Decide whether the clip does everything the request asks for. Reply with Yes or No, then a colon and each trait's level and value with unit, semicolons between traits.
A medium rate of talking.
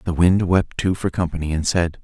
No: fast, 235 wpm